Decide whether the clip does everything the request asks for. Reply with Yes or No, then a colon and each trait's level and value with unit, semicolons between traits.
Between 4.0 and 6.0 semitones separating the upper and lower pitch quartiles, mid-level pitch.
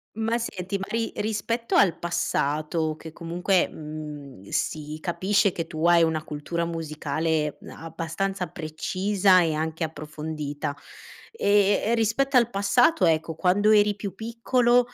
Yes: average, 4.8 semitones; medium, 175 Hz